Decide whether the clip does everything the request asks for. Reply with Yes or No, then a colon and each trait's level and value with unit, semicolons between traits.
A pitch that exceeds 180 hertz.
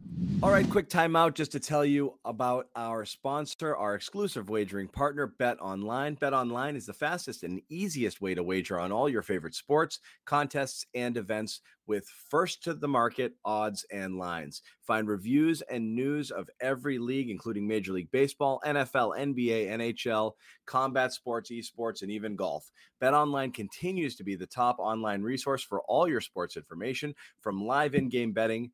No: low, 125 Hz